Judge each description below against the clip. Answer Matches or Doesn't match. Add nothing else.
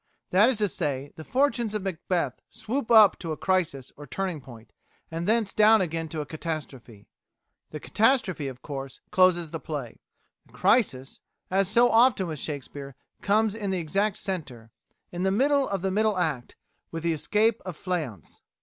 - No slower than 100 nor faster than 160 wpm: Doesn't match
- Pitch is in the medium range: Matches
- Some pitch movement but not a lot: Doesn't match